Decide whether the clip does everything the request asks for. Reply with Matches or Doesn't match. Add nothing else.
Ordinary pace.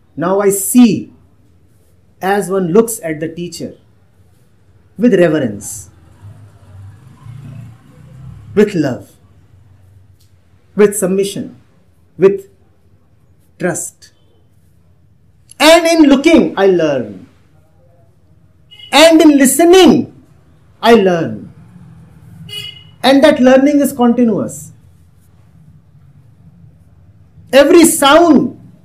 Doesn't match